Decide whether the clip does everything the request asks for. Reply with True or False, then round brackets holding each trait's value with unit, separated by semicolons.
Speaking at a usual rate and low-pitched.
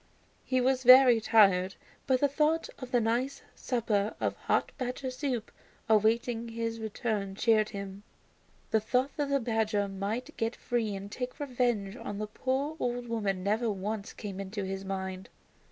False (160 wpm; 225 Hz)